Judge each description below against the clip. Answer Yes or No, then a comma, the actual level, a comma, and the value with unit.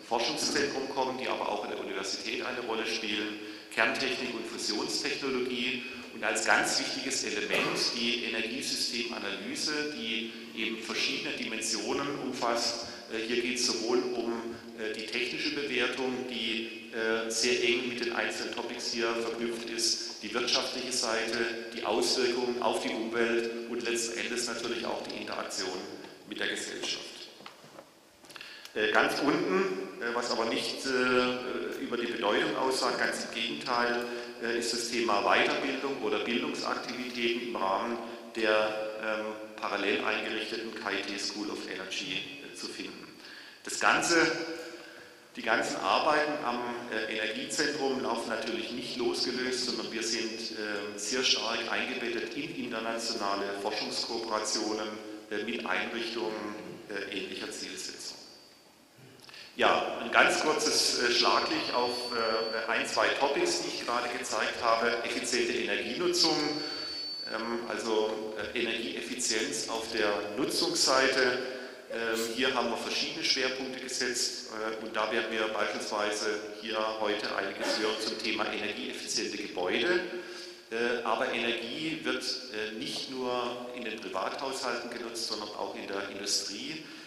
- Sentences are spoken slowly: Yes, slow, 120 wpm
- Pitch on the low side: Yes, low, 115 Hz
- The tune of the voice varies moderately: No, narrow, 2.3 semitones